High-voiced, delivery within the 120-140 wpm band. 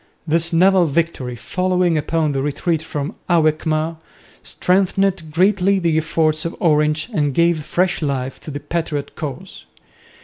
No: medium, 165 Hz; slow, 135 wpm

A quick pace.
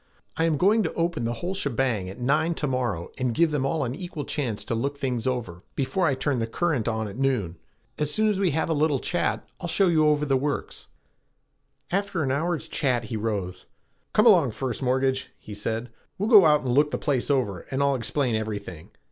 Yes: fast, 220 wpm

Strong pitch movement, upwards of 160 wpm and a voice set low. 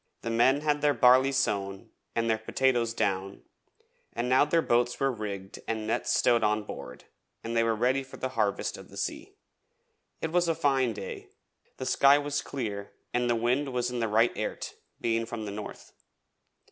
No: average, 3.3 semitones; average, 185 wpm; low, 120 Hz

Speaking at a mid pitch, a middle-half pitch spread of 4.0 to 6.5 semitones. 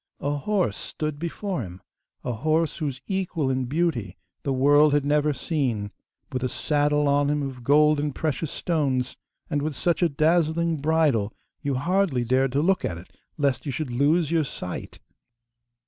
No: medium, 145 Hz; average, 3.4 semitones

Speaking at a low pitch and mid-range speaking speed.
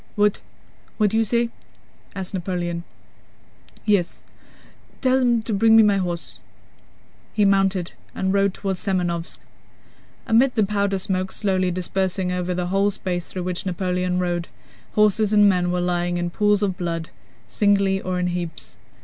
No: high, 190 Hz; average, 150 wpm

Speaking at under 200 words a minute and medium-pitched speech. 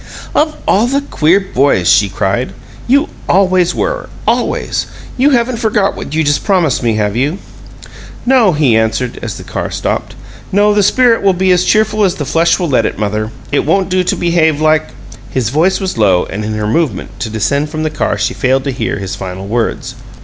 No: fast, 205 wpm; medium, 155 Hz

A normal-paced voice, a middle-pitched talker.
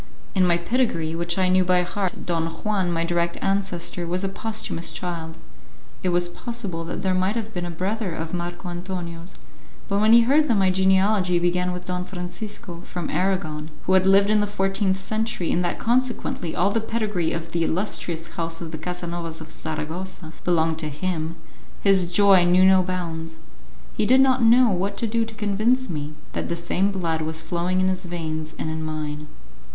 Yes: average, 190 wpm; medium, 180 Hz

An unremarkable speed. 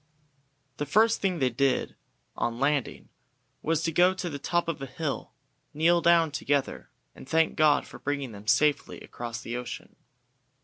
Yes: average, 165 wpm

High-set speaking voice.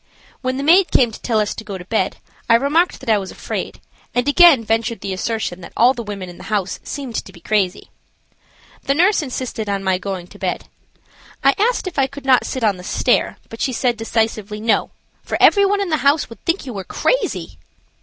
Yes: high, 230 Hz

